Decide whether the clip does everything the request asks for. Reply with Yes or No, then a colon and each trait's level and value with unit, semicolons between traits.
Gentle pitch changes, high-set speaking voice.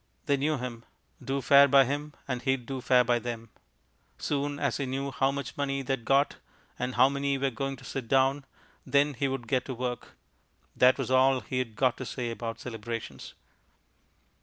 No: narrow, 2.0 semitones; low, 135 Hz